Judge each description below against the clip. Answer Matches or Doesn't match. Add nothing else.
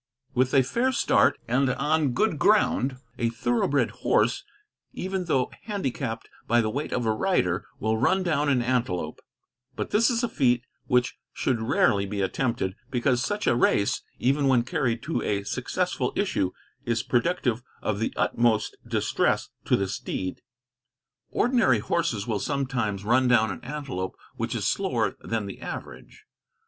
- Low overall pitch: Matches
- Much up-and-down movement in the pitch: Doesn't match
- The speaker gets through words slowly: Doesn't match